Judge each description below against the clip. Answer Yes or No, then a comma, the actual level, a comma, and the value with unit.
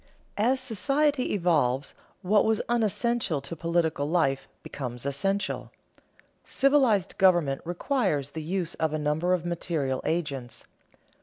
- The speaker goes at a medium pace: No, slow, 120 wpm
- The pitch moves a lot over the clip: Yes, wide, 6.4 semitones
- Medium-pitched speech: Yes, medium, 170 Hz